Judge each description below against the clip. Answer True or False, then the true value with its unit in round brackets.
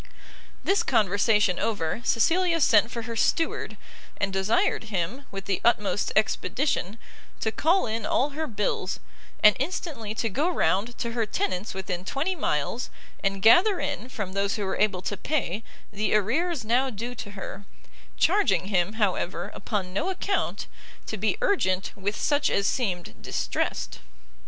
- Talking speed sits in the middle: True (150 wpm)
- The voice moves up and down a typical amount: False (5.8 semitones)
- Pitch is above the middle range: True (220 Hz)